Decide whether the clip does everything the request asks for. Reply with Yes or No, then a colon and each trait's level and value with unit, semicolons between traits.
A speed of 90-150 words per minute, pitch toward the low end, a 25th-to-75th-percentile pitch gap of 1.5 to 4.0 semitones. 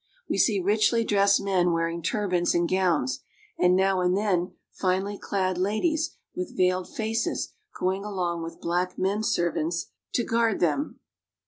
No: average, 145 wpm; medium, 185 Hz; average, 2.8 semitones